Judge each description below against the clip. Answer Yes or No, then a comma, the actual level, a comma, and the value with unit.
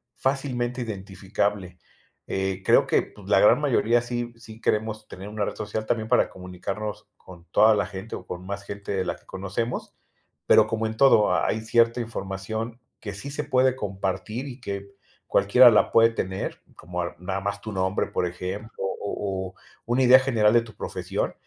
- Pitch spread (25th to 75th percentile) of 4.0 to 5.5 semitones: No, average, 3.3 semitones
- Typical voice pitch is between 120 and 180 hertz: No, low, 105 Hz